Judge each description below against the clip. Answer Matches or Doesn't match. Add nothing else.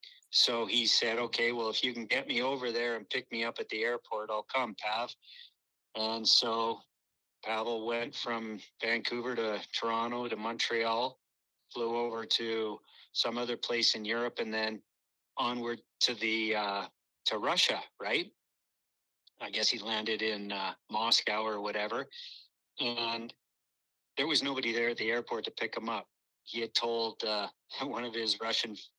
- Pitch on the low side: Matches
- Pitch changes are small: Matches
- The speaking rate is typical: Matches